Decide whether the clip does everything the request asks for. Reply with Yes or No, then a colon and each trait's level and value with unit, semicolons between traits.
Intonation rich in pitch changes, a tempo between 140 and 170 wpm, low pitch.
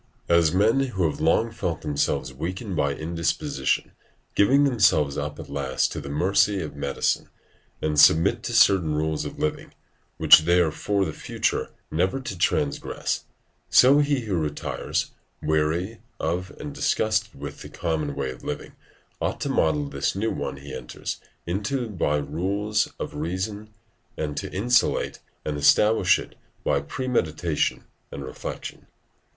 Yes: wide, 5.8 semitones; average, 150 wpm; very low, 85 Hz